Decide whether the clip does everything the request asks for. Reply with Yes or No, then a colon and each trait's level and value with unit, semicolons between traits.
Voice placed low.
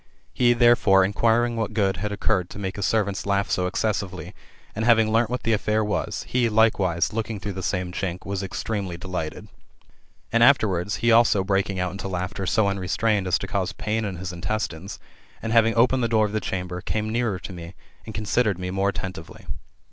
Yes: low, 100 Hz